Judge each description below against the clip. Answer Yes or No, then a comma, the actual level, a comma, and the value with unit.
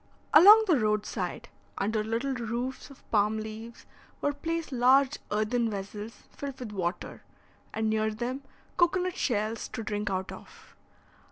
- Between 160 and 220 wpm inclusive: No, average, 150 wpm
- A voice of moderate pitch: No, high, 230 Hz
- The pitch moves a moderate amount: Yes, average, 4.3 semitones